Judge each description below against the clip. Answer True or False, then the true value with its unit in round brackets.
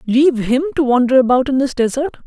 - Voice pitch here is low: False (265 Hz)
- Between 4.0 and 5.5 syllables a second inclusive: False (6.2 syllables/s)